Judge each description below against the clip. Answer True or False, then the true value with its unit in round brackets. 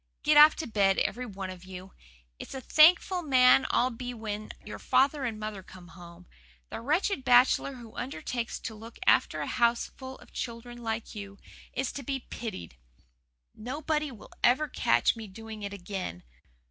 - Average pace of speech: True (170 wpm)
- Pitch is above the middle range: True (235 Hz)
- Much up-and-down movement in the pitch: False (4.7 semitones)